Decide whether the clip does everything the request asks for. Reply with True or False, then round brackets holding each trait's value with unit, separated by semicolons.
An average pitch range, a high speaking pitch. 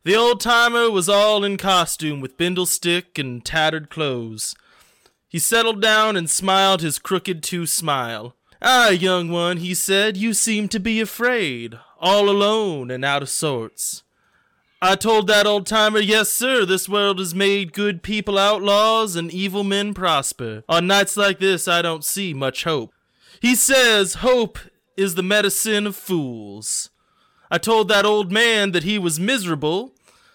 True (4.0 semitones; 195 Hz)